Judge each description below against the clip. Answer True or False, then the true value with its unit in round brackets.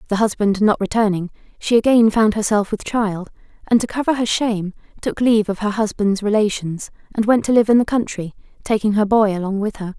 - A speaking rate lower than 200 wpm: False (205 wpm)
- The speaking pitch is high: True (210 Hz)